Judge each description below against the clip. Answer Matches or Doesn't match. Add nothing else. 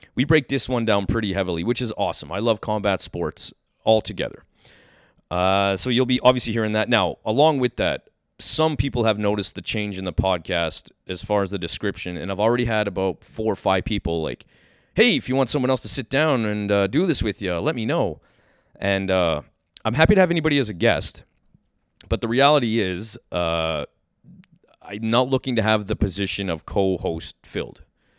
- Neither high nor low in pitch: Doesn't match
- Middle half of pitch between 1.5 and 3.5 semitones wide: Doesn't match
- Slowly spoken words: Doesn't match